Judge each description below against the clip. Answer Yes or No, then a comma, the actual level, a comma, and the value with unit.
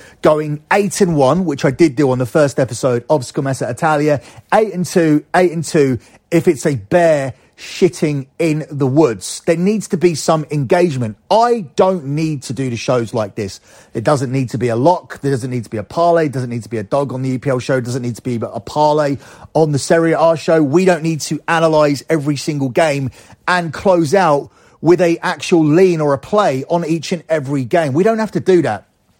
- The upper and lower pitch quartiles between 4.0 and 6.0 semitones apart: Yes, average, 4.3 semitones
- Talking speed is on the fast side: Yes, fast, 225 wpm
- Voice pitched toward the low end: No, medium, 150 Hz